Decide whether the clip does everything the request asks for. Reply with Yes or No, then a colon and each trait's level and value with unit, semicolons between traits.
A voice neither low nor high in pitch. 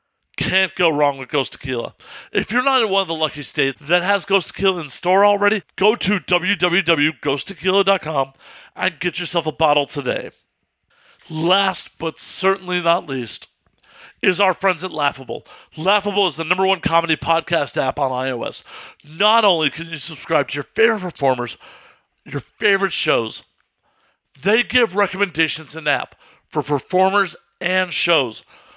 Yes: medium, 175 Hz